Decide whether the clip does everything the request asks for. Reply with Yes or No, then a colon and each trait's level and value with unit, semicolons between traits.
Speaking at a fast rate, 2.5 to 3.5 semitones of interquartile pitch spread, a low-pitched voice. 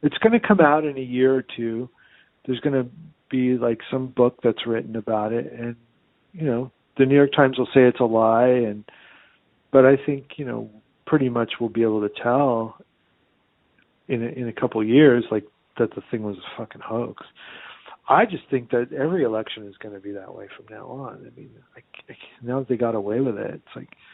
Yes: fast, 220 wpm; average, 2.8 semitones; low, 125 Hz